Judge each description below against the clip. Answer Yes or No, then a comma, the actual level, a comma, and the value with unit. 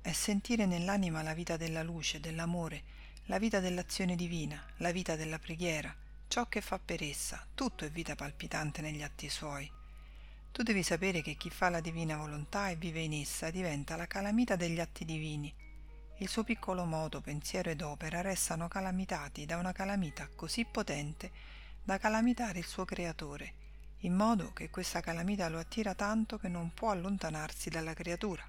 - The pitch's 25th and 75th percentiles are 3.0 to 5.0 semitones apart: Yes, average, 3.8 semitones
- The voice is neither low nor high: Yes, medium, 170 Hz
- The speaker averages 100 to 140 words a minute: No, fast, 170 wpm